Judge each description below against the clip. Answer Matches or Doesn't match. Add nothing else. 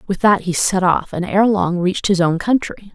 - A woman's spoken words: Matches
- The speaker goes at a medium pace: Doesn't match